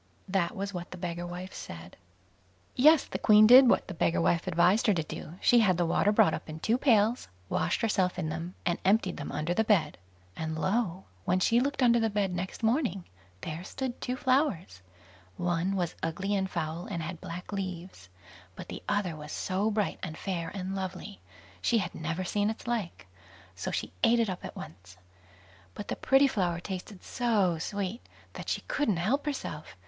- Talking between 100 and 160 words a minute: No, average, 195 wpm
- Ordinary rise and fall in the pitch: Yes, average, 4.3 semitones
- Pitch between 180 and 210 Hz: Yes, medium, 185 Hz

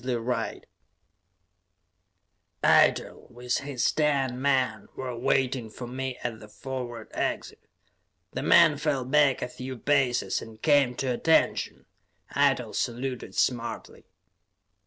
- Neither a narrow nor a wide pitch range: No, narrow, 2.1 semitones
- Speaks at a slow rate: Yes, slow, 110 wpm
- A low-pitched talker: Yes, low, 130 Hz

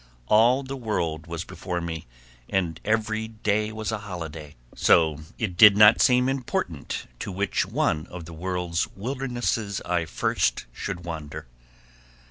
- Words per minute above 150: No, average, 140 wpm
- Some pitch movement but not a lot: Yes, average, 4.9 semitones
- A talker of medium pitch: No, very low, 95 Hz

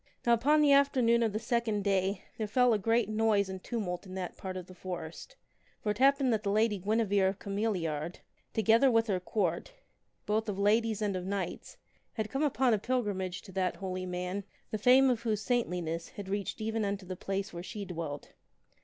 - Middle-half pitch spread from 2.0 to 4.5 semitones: Yes, average, 3.5 semitones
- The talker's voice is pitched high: Yes, high, 205 Hz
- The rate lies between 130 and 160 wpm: No, fast, 205 wpm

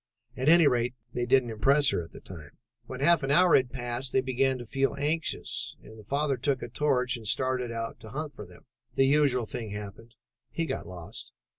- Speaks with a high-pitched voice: No, low, 130 Hz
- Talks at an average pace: No, fast, 210 wpm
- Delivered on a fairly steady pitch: No, average, 3.5 semitones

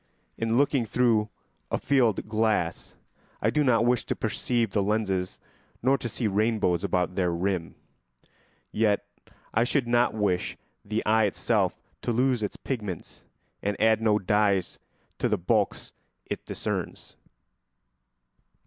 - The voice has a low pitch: Yes, low, 110 Hz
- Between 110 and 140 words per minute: Yes, slow, 135 wpm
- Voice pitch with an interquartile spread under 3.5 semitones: Yes, average, 3.0 semitones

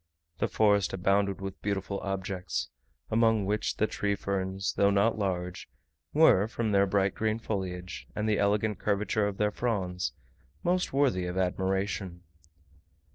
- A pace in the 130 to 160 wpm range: Yes, average, 140 wpm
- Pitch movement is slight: Yes, narrow, 2.0 semitones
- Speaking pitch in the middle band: No, low, 100 Hz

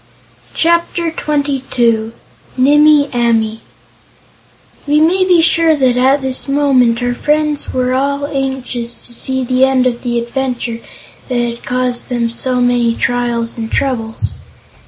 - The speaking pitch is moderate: No, very high, 255 Hz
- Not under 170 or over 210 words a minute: No, slow, 135 wpm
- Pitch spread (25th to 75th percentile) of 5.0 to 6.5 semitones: No, average, 3.1 semitones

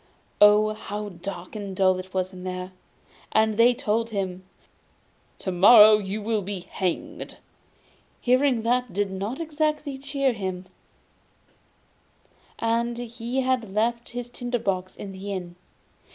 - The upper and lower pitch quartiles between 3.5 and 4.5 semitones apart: Yes, average, 4.2 semitones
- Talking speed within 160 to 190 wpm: No, slow, 135 wpm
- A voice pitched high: Yes, high, 210 Hz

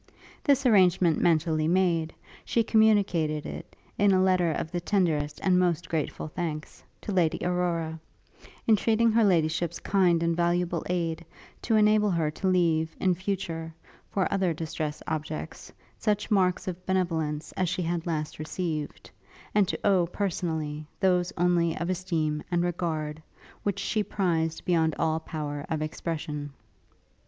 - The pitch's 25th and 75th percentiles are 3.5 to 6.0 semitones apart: No, average, 2.7 semitones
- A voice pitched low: No, medium, 170 Hz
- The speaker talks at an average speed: Yes, average, 145 wpm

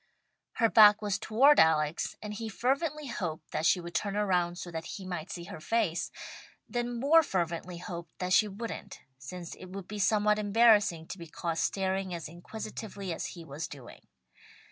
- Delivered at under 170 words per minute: No, average, 180 wpm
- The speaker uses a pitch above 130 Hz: Yes, high, 190 Hz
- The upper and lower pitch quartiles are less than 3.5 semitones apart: No, average, 4.0 semitones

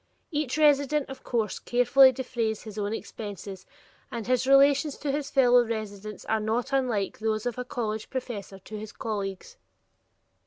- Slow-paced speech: No, average, 155 wpm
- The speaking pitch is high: Yes, high, 235 Hz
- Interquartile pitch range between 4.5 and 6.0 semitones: No, average, 3.9 semitones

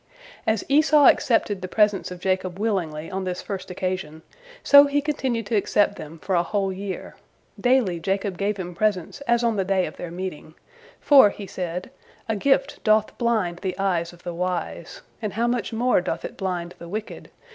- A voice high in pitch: Yes, high, 195 Hz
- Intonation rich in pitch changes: No, average, 3.8 semitones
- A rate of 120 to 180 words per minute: No, average, 190 wpm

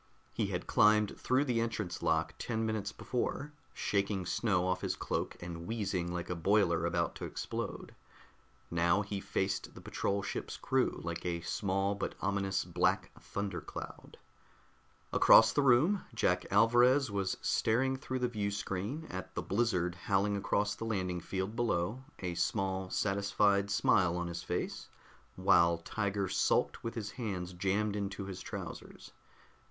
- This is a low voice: Yes, low, 100 Hz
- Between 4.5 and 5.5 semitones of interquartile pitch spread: No, average, 3.4 semitones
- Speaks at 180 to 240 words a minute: No, average, 145 wpm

